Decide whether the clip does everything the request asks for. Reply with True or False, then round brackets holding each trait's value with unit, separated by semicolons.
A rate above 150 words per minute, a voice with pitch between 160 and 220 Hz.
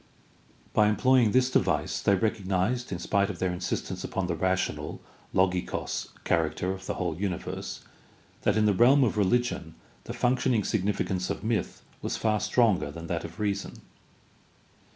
False (160 wpm; 100 Hz)